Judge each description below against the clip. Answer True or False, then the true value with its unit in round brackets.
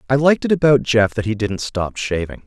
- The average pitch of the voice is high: False (120 Hz)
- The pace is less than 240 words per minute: False (245 wpm)